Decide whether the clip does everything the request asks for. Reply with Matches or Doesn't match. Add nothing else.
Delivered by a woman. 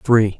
Doesn't match